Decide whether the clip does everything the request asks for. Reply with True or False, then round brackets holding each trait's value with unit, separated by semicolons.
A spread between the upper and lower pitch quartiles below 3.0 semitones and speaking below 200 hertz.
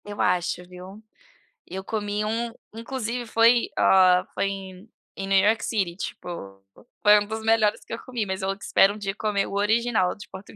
False (2.6 semitones; 205 Hz)